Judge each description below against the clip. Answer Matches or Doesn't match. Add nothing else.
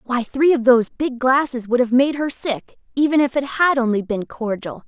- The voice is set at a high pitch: Matches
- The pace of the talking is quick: Matches